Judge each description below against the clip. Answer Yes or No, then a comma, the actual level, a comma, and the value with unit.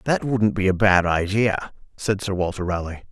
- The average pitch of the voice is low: Yes, low, 100 Hz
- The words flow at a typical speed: Yes, average, 195 wpm